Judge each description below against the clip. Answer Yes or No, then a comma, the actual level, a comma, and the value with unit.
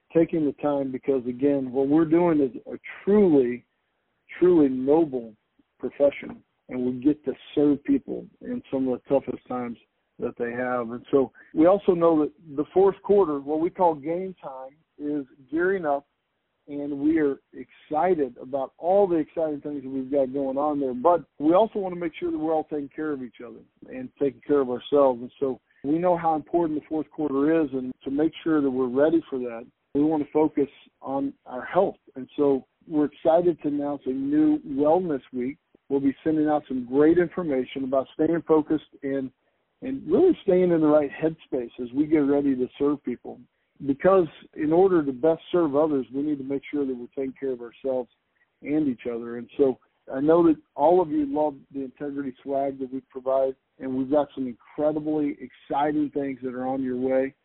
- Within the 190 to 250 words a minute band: Yes, average, 200 wpm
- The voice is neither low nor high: Yes, medium, 145 Hz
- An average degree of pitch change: Yes, average, 3.3 semitones